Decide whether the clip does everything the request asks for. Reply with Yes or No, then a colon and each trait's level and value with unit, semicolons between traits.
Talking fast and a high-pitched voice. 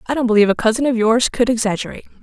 Yes: fast, 240 wpm; high, 235 Hz